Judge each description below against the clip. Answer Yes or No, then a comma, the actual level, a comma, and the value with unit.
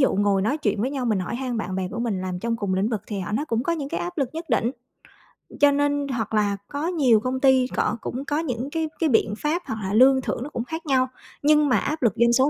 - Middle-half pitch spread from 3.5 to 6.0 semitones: Yes, average, 4.9 semitones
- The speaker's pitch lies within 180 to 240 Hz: No, very high, 250 Hz